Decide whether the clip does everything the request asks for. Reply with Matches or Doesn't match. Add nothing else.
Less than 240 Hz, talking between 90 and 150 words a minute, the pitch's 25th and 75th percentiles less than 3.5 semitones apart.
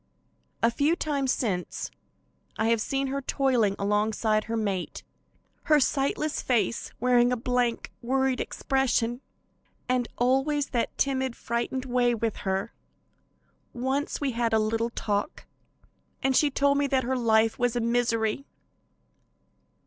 Doesn't match